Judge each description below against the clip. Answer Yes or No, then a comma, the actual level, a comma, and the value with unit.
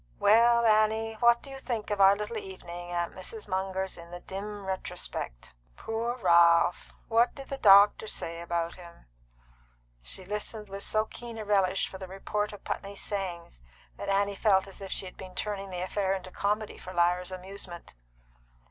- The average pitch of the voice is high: Yes, high, 195 Hz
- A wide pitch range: No, average, 2.7 semitones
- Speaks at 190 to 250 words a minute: No, average, 175 wpm